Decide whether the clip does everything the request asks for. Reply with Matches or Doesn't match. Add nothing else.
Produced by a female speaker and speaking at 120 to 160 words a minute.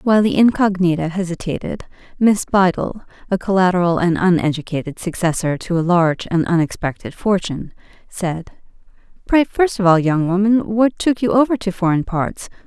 Matches